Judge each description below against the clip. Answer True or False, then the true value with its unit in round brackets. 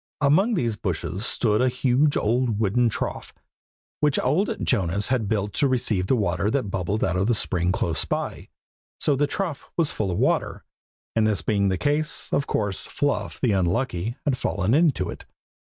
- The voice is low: True (110 Hz)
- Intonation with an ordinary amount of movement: False (6.1 semitones)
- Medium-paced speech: True (180 wpm)